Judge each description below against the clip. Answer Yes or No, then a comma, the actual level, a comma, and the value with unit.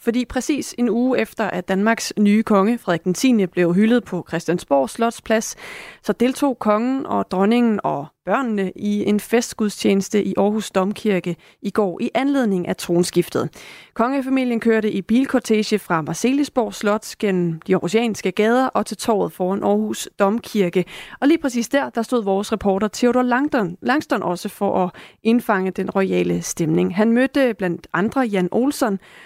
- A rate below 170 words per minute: Yes, average, 155 wpm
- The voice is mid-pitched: No, high, 210 Hz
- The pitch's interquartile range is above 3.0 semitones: Yes, average, 4.3 semitones